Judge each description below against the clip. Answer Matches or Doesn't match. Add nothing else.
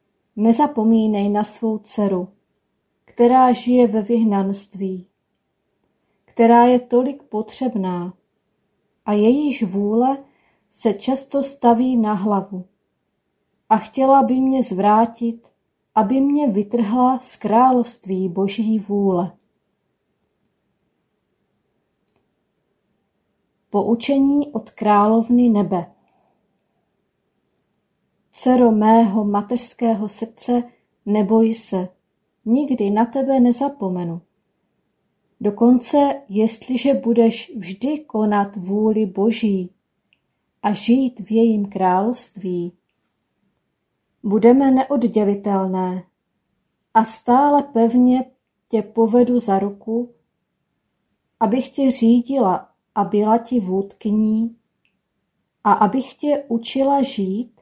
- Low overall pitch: Doesn't match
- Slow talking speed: Matches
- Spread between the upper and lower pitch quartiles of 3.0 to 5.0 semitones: Matches